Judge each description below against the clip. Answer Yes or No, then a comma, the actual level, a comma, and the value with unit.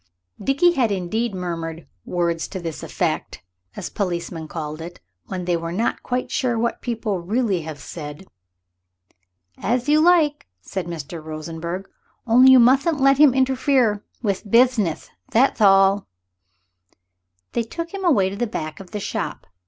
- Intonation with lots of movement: Yes, wide, 6.8 semitones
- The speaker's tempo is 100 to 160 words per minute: Yes, average, 150 wpm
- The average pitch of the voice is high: Yes, high, 200 Hz